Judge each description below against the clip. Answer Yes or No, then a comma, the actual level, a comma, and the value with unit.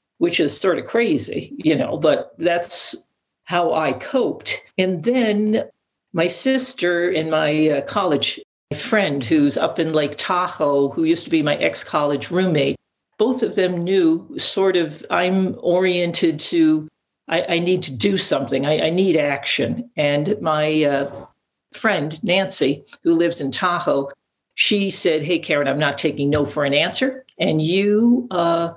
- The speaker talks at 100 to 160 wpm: Yes, average, 155 wpm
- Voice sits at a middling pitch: Yes, medium, 175 Hz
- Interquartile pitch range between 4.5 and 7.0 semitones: Yes, average, 4.8 semitones